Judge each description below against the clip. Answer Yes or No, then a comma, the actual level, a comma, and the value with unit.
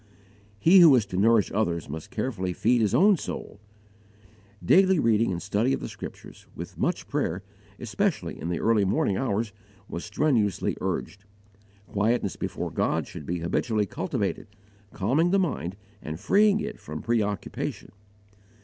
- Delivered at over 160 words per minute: No, average, 150 wpm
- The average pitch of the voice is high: No, low, 105 Hz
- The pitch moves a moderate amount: No, wide, 5.9 semitones